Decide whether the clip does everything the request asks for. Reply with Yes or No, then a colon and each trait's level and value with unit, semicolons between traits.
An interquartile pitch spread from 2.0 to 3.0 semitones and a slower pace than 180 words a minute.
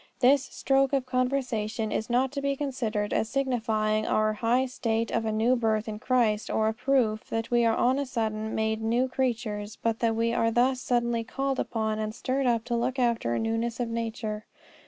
No: narrow, 2.6 semitones; average, 200 wpm